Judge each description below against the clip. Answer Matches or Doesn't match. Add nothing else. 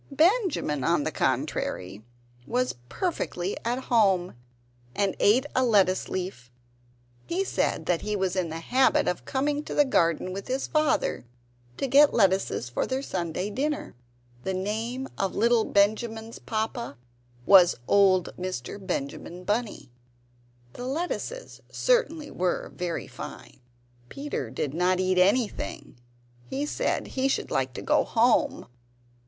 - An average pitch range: Doesn't match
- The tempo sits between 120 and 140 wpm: Matches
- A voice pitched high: Matches